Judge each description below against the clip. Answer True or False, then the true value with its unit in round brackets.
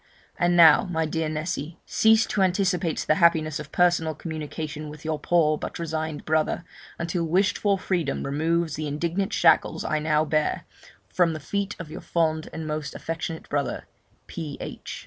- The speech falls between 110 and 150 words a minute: False (165 wpm)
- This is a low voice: False (160 Hz)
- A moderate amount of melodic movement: False (2.1 semitones)